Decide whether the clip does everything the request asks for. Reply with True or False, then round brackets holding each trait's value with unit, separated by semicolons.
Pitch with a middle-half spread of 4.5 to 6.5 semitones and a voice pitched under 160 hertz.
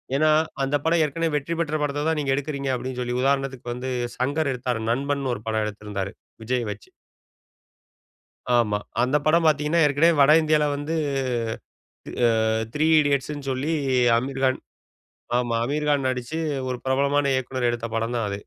False (3.2 semitones; 135 Hz)